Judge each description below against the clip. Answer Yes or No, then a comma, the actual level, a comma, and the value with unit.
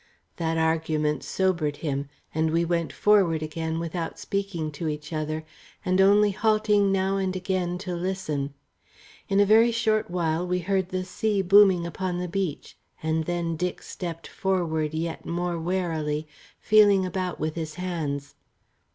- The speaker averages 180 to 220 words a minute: No, average, 150 wpm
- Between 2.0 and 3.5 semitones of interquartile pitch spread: Yes, average, 3.2 semitones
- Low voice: No, medium, 175 Hz